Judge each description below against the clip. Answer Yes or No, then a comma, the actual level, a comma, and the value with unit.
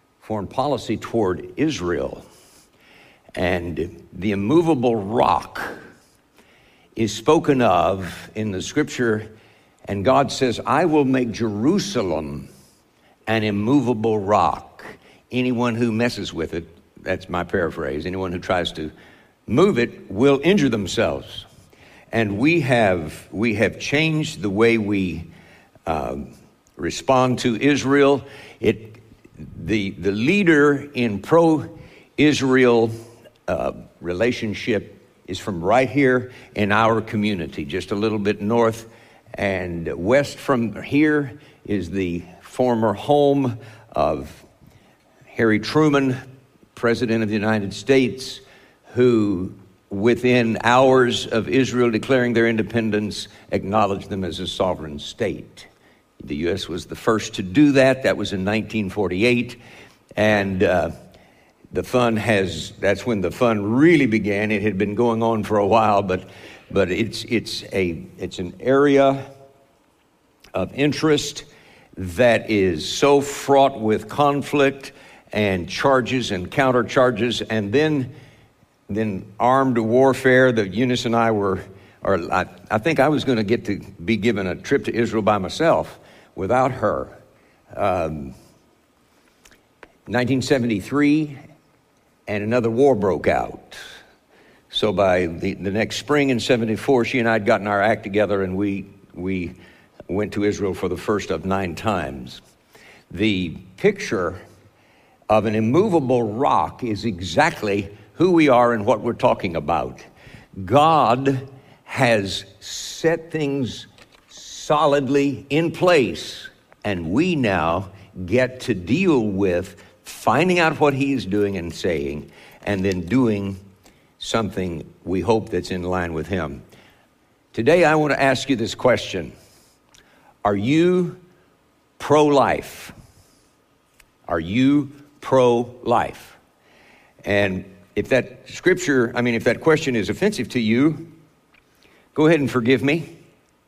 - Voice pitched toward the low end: Yes, low, 115 Hz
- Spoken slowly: Yes, slow, 125 wpm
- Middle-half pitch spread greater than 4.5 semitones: Yes, average, 4.9 semitones